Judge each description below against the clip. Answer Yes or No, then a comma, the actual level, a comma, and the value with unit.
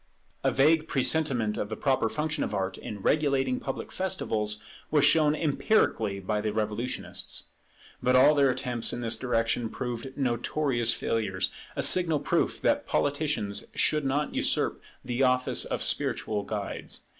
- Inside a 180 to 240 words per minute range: No, average, 145 wpm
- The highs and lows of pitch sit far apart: No, average, 4.9 semitones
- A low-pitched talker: Yes, low, 125 Hz